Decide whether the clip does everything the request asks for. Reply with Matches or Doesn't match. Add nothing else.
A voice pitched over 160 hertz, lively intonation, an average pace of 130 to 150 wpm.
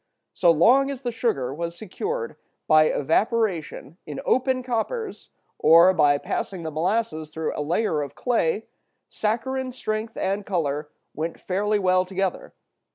Matches